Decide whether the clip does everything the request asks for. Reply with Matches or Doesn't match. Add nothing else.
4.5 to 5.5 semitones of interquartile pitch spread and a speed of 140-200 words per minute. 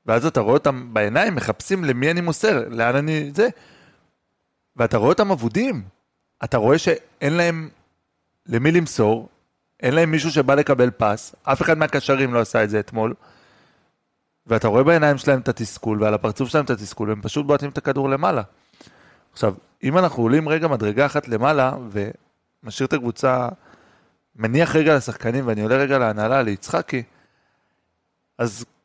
Matches